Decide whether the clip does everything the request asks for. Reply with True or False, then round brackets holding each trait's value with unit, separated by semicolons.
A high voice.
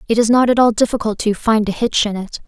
True (220 Hz)